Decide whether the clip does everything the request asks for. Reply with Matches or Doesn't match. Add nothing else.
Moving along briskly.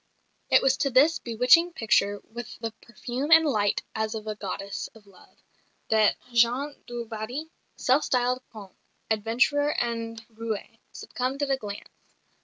Doesn't match